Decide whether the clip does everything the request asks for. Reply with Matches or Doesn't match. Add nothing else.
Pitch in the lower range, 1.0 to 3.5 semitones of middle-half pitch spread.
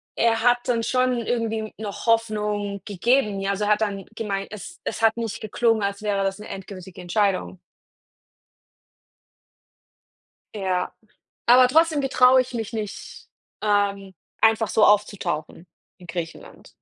Doesn't match